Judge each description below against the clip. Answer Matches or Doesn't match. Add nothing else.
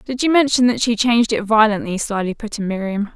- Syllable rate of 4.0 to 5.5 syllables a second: Doesn't match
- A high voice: Matches